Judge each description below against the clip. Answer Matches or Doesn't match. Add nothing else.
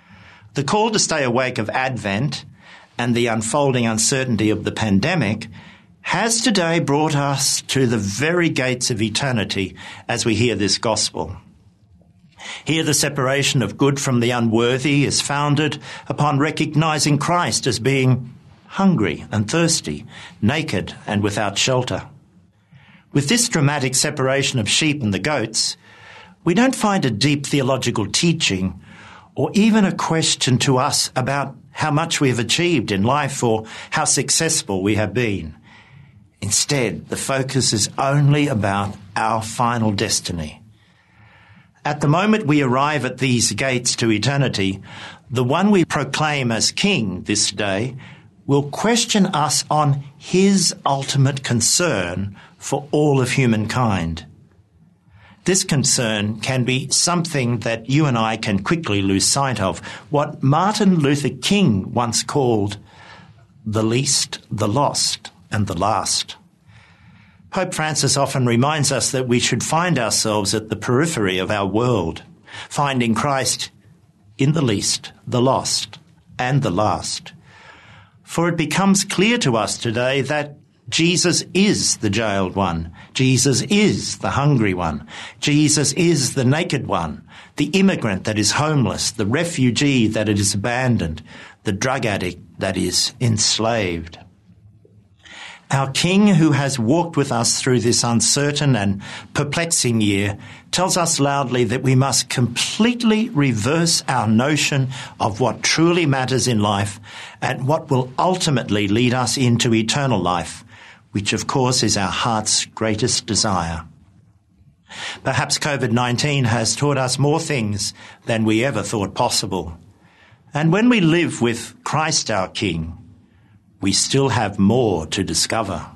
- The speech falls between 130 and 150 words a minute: Matches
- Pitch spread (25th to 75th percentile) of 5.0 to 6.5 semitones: Matches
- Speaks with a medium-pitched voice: Doesn't match